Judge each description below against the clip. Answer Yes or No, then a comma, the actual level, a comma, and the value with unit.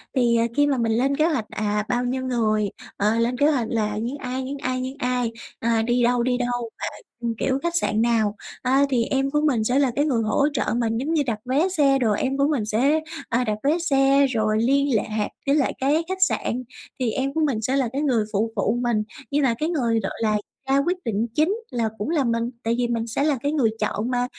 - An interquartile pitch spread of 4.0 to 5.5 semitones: No, average, 3.5 semitones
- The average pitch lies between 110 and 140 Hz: No, very high, 250 Hz